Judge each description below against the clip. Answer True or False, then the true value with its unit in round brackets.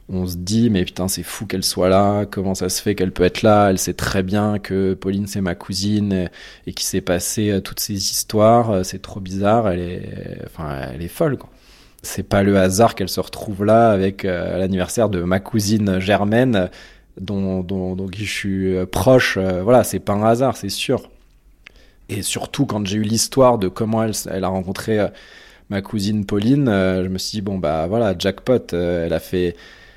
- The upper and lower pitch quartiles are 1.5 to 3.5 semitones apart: True (2.4 semitones)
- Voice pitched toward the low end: True (100 Hz)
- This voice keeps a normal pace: True (195 wpm)